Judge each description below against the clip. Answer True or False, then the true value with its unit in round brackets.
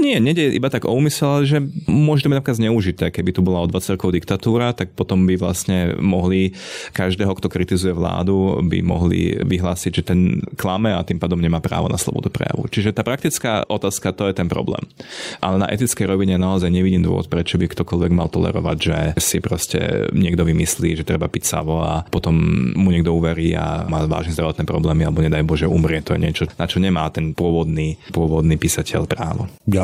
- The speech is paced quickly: True (190 wpm)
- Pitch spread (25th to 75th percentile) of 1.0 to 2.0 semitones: False (2.7 semitones)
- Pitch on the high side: False (90 Hz)